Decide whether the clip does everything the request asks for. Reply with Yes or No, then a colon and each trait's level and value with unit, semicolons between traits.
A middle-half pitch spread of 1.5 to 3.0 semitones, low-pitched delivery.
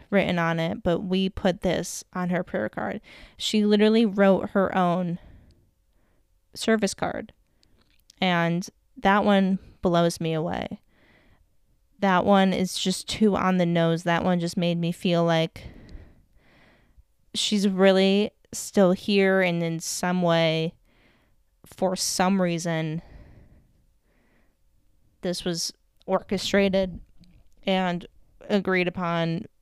No: narrow, 2.5 semitones; medium, 180 Hz